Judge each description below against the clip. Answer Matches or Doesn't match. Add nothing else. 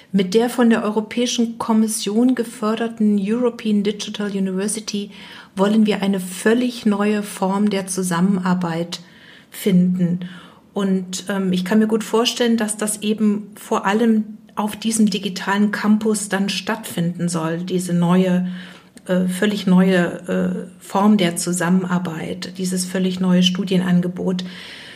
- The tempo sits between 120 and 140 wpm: Matches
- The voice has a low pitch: Doesn't match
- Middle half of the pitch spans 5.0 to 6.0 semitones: Doesn't match